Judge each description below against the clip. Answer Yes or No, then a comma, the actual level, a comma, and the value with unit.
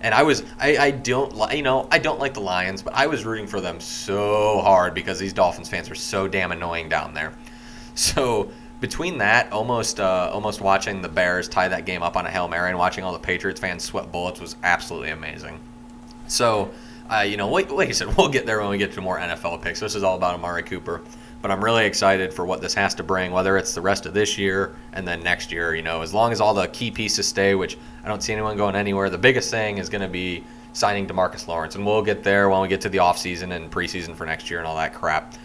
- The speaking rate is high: Yes, fast, 250 wpm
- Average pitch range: Yes, average, 3.6 semitones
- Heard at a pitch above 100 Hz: No, very low, 95 Hz